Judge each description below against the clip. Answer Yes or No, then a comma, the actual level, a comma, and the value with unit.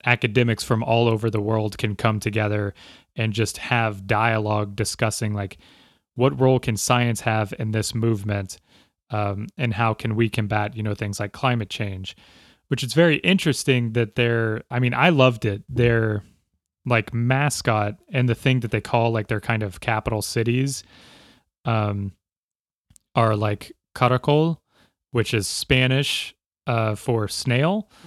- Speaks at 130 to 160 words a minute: Yes, average, 150 wpm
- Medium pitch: No, low, 115 Hz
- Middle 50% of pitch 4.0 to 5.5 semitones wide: No, average, 2.8 semitones